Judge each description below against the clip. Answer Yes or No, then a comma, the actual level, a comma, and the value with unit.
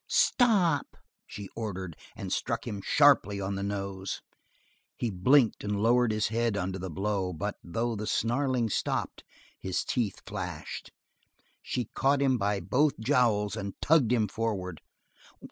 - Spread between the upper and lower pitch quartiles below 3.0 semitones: No, average, 4.1 semitones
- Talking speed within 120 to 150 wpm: Yes, average, 145 wpm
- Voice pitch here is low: Yes, low, 110 Hz